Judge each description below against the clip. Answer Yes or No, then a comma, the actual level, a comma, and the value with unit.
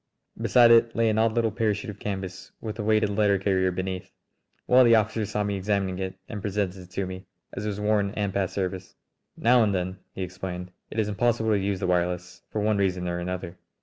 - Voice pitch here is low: Yes, low, 100 Hz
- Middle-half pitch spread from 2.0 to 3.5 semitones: Yes, narrow, 2.6 semitones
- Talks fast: Yes, fast, 225 wpm